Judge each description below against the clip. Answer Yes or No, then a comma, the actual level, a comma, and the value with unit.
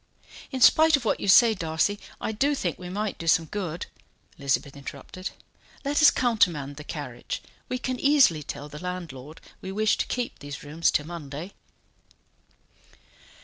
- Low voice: No, medium, 180 Hz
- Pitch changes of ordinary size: No, wide, 7.0 semitones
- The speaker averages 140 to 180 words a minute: Yes, average, 160 wpm